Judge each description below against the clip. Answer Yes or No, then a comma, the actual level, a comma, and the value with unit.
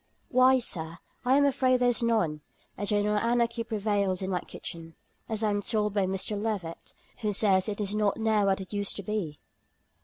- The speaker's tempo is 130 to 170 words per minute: No, average, 195 wpm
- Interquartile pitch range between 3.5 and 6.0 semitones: No, average, 2.9 semitones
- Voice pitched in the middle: No, high, 210 Hz